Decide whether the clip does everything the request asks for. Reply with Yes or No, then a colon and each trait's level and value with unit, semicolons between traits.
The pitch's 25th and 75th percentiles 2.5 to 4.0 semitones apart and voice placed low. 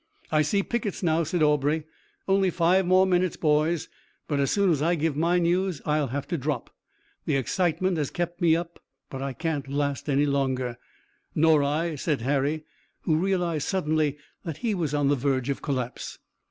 No: average, 3.6 semitones; medium, 155 Hz